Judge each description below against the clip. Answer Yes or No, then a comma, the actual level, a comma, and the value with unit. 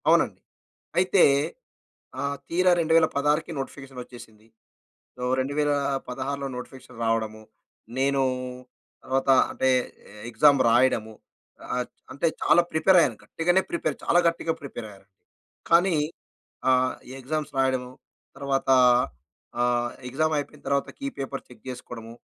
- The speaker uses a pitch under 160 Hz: Yes, low, 135 Hz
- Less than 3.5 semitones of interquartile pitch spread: No, average, 3.8 semitones